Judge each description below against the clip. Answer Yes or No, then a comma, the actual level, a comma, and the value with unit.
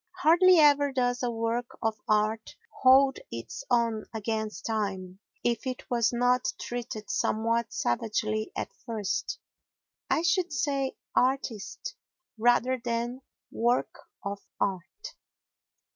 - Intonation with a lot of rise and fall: No, average, 3.0 semitones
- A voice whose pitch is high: Yes, high, 235 Hz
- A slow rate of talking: Yes, slow, 110 wpm